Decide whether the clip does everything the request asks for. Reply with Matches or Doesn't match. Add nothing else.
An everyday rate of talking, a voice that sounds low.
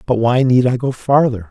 Doesn't match